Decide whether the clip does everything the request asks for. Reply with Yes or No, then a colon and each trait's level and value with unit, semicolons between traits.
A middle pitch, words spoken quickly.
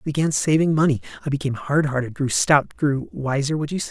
Yes: medium, 145 Hz; fast, 215 wpm